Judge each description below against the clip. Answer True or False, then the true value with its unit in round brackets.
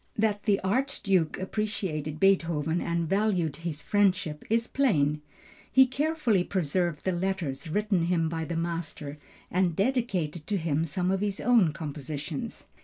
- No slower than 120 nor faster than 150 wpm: True (140 wpm)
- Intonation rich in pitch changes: False (4.4 semitones)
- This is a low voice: False (180 Hz)